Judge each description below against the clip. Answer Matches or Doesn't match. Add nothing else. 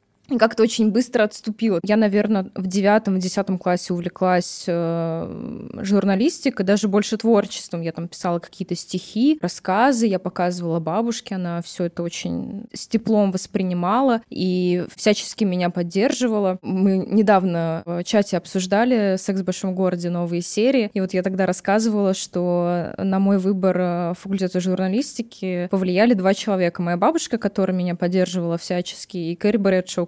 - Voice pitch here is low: Doesn't match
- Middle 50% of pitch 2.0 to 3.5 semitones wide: Matches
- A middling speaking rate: Matches